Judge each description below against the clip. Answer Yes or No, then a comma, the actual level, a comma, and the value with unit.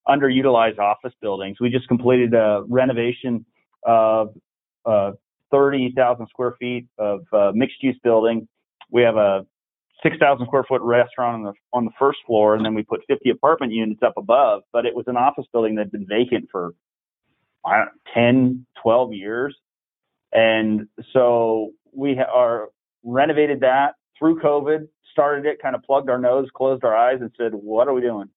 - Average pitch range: Yes, average, 3.0 semitones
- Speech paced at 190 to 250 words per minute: No, average, 175 wpm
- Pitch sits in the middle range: No, low, 120 Hz